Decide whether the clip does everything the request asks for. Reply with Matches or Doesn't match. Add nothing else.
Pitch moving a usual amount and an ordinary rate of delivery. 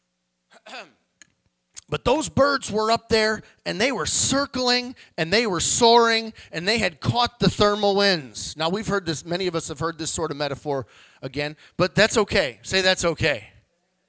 Doesn't match